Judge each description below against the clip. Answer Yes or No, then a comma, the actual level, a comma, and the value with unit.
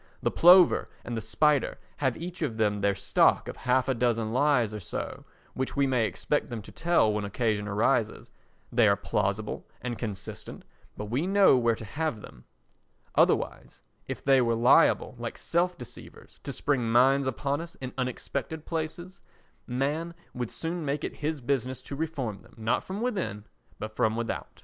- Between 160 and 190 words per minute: Yes, average, 175 wpm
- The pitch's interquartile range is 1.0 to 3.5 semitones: No, average, 5.3 semitones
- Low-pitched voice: Yes, low, 125 Hz